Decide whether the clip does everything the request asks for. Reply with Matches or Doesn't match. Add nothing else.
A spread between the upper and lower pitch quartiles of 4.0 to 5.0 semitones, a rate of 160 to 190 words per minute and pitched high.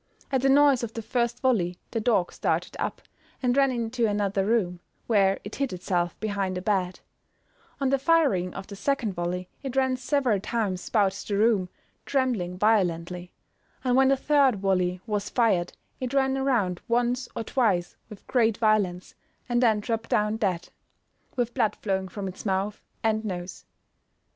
Matches